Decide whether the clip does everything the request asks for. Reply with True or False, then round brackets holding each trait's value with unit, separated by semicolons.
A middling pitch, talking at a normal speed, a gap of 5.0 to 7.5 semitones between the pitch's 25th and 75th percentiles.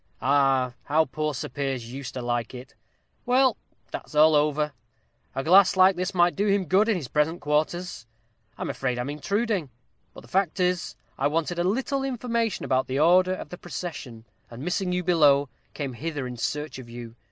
True (155 Hz; 185 wpm; 5.4 semitones)